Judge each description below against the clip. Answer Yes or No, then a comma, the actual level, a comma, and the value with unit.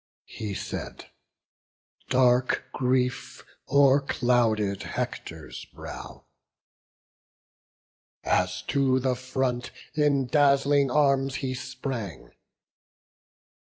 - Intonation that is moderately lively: No, narrow, 2.1 semitones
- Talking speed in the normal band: No, slow, 70 wpm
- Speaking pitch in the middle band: No, low, 130 Hz